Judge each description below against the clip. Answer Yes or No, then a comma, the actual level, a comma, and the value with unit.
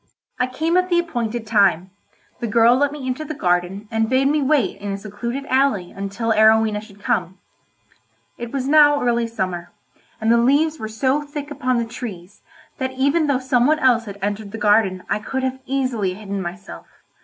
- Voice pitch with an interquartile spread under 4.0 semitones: No, average, 4.8 semitones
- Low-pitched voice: No, high, 235 Hz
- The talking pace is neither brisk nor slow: Yes, average, 190 wpm